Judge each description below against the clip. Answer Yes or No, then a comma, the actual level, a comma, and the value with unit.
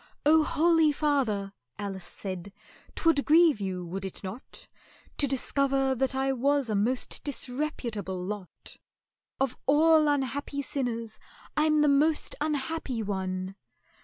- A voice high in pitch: Yes, very high, 265 Hz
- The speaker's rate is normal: No, slow, 130 wpm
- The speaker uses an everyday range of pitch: No, wide, 6.5 semitones